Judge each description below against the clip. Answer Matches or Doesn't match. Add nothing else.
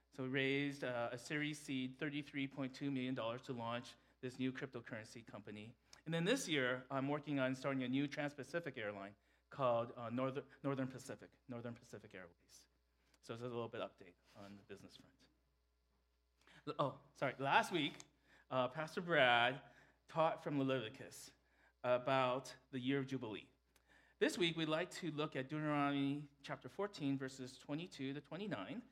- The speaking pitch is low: Matches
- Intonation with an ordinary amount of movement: Matches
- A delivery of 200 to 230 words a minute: Doesn't match